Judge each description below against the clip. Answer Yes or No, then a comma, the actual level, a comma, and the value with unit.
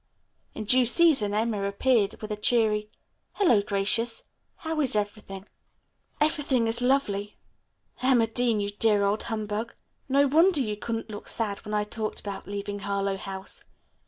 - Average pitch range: Yes, average, 3.3 semitones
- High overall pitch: Yes, high, 215 Hz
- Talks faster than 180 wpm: No, average, 150 wpm